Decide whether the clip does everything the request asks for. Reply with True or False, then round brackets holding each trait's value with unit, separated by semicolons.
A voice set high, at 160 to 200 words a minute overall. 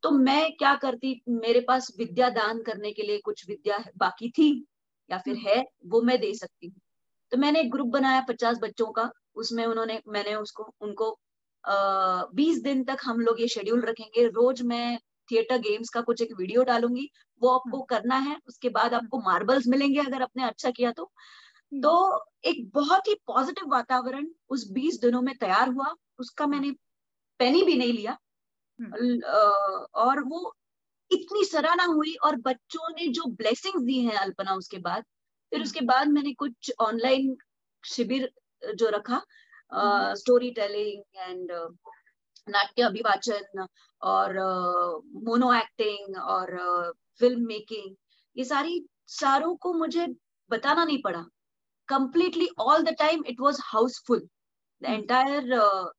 False (250 Hz; 145 wpm)